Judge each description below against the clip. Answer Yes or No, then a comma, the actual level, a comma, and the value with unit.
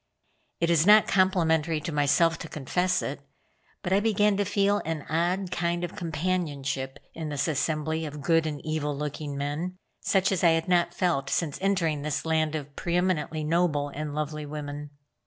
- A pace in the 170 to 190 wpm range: Yes, average, 175 wpm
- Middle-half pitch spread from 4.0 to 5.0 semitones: No, average, 3.1 semitones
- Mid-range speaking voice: Yes, medium, 160 Hz